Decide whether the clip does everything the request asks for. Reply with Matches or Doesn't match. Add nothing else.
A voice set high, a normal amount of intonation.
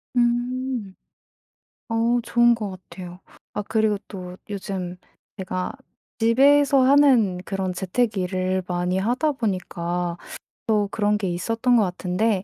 Matches